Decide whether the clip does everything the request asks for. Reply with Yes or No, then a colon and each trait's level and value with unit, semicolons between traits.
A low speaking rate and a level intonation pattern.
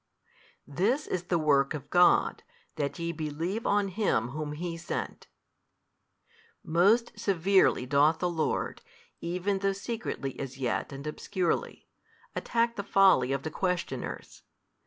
No: slow, 130 wpm; average, 4.8 semitones